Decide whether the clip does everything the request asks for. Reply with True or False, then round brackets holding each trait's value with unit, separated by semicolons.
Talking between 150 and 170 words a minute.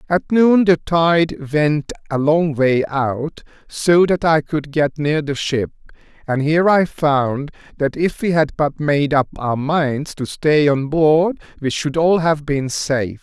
False (180 wpm)